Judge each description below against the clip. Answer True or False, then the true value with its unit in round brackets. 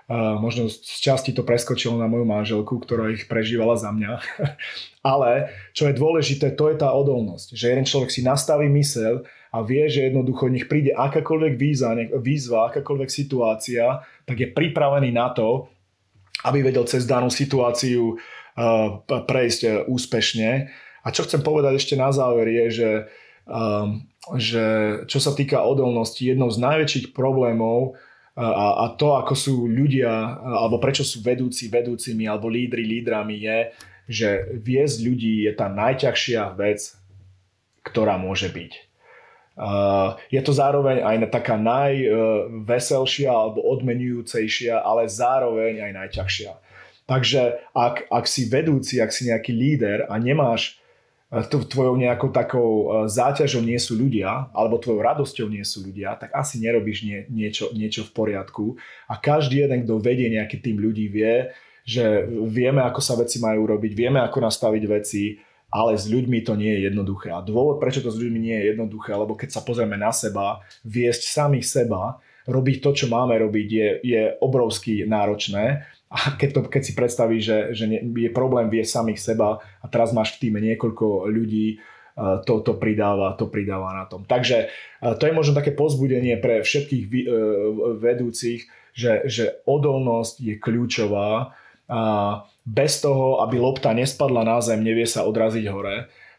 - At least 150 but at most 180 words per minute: True (155 wpm)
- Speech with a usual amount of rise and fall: True (3.1 semitones)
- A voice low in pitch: True (115 Hz)